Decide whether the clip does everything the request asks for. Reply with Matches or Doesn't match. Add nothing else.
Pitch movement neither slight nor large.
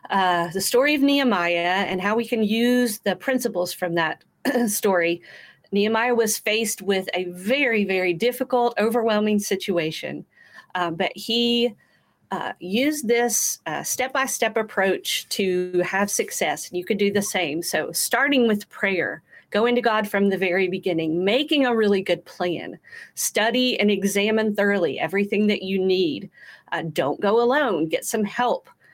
Matches